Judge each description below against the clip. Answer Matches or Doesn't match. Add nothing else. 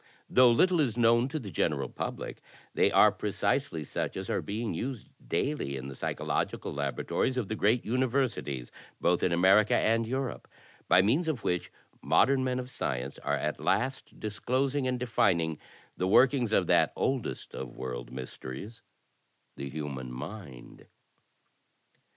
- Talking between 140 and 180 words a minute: Matches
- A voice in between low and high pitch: Doesn't match